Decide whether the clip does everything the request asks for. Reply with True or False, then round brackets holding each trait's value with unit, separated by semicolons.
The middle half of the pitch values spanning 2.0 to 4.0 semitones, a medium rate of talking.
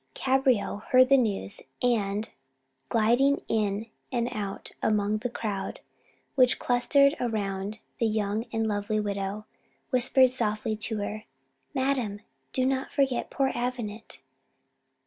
False (3.5 semitones; 120 wpm)